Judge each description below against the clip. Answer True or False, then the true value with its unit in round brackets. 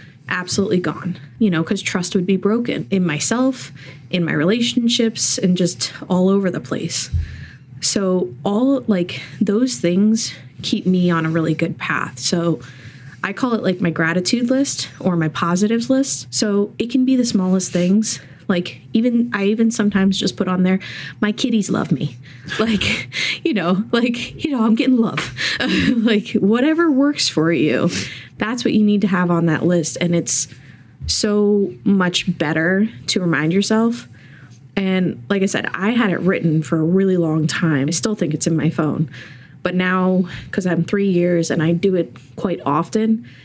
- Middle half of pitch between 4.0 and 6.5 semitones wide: True (5.1 semitones)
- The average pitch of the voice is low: False (185 Hz)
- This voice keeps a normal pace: True (175 wpm)